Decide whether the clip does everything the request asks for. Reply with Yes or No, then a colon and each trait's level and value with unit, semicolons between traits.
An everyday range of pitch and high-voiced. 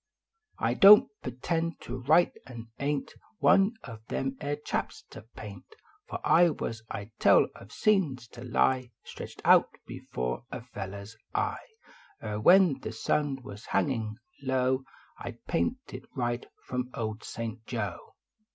No: average, 4.7 semitones; low, 125 Hz